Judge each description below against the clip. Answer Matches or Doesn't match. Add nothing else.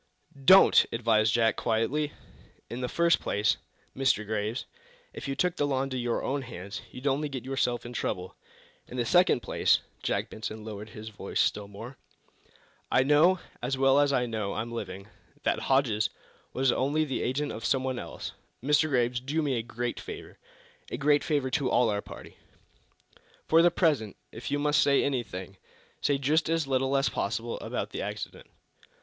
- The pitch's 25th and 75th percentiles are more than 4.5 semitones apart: Doesn't match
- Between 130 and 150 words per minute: Doesn't match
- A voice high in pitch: Doesn't match